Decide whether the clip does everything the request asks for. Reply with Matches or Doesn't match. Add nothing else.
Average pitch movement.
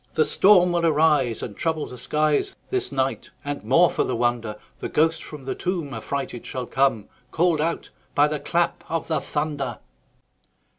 Matches